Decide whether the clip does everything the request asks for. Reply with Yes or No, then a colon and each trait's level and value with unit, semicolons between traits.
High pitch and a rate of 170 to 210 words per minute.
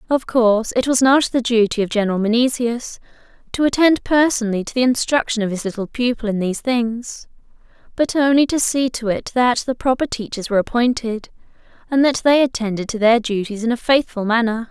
Yes: high, 240 Hz; average, 190 wpm